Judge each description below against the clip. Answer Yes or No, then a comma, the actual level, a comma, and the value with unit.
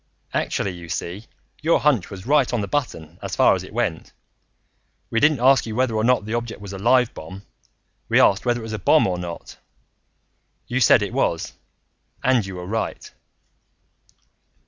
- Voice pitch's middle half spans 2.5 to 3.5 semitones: No, average, 4.8 semitones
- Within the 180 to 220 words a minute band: Yes, average, 185 wpm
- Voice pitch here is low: Yes, low, 110 Hz